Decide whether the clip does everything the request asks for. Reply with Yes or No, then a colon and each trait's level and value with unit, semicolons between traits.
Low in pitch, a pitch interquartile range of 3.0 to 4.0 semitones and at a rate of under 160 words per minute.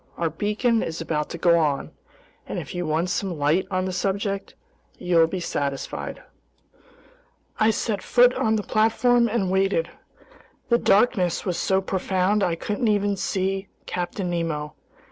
No: high, 190 Hz; average, 3.6 semitones; average, 150 wpm